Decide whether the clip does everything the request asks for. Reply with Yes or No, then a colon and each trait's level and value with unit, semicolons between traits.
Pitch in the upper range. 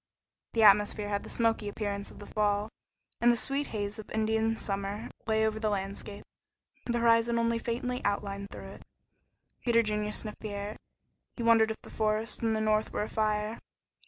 Yes: high, 215 Hz